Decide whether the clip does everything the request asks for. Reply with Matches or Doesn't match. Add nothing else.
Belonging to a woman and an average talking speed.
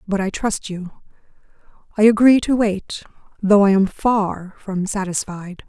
Matches